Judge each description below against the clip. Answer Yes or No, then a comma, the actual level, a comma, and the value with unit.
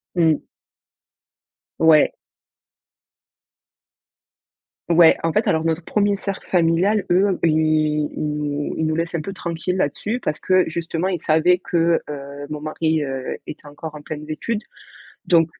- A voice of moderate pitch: Yes, medium, 160 Hz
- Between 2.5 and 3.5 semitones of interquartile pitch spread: Yes, average, 2.8 semitones